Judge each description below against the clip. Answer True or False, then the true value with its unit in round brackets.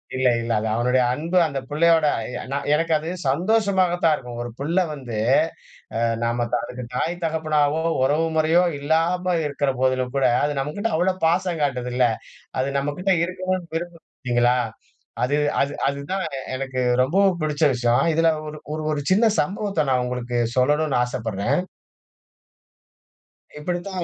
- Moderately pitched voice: True (150 Hz)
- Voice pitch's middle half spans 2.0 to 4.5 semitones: False (5.1 semitones)